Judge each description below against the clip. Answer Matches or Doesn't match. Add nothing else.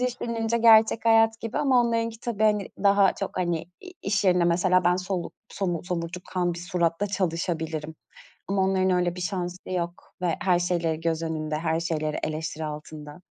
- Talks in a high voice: Doesn't match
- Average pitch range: Matches